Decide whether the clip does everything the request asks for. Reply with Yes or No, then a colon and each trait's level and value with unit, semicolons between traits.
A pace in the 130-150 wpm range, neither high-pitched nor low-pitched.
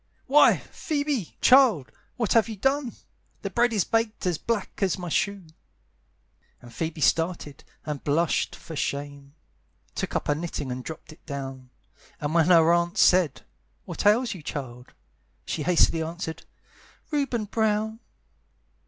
Yes: average, 145 wpm; medium, 175 Hz